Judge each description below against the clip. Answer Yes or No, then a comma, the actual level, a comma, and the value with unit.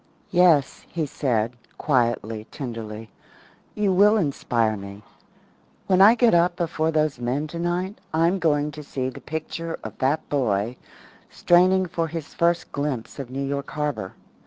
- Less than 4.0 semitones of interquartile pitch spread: No, wide, 5.5 semitones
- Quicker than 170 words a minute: No, average, 145 wpm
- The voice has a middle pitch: Yes, medium, 150 Hz